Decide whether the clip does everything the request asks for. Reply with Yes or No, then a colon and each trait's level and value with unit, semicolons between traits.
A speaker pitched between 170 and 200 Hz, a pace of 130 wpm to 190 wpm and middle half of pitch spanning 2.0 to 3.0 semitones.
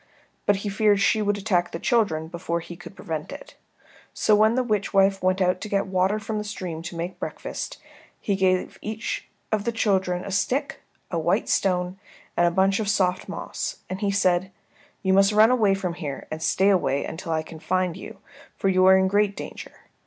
No: high, 190 Hz; fast, 205 wpm; narrow, 2.5 semitones